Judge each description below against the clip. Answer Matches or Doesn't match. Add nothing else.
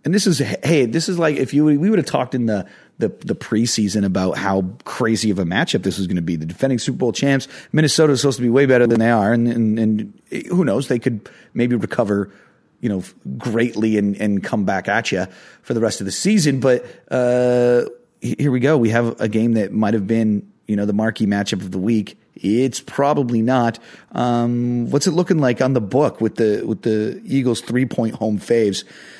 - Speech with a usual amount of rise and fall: Matches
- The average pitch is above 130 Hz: Doesn't match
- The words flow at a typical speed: Doesn't match